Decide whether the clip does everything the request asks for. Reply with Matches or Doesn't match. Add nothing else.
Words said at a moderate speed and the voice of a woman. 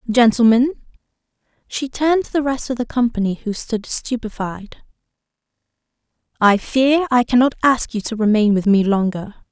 Doesn't match